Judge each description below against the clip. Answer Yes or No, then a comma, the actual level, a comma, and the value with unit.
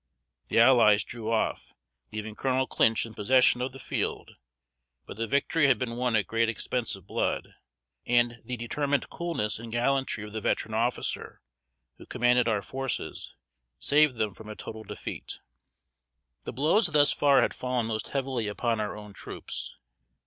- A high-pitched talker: No, low, 120 Hz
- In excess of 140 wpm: Yes, average, 165 wpm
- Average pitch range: Yes, average, 3.3 semitones